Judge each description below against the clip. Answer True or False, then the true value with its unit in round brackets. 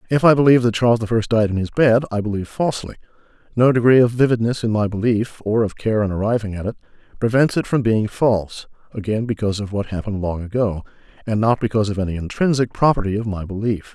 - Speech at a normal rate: False (215 wpm)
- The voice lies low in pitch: True (110 Hz)